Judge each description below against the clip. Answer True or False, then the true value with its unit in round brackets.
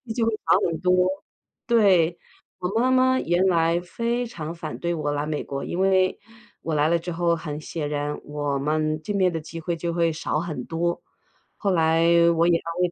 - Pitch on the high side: False (170 Hz)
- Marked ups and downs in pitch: False (2.7 semitones)